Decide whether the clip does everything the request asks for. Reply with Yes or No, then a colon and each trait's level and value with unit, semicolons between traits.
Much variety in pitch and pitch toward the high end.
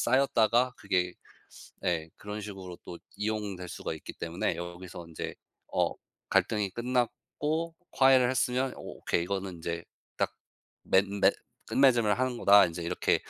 No: wide, 5.8 semitones; low, 100 Hz